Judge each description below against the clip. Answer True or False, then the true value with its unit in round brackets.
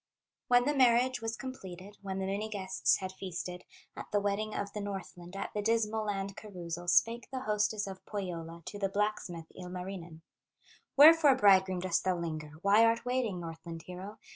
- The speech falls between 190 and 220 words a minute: False (170 wpm)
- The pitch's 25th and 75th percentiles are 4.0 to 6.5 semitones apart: False (3.3 semitones)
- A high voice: True (195 Hz)